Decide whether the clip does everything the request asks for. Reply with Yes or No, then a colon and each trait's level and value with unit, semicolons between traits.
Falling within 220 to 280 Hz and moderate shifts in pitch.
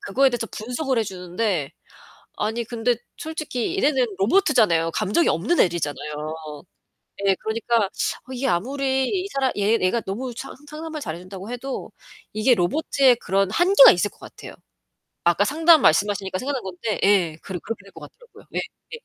No: high, 230 Hz; wide, 6.1 semitones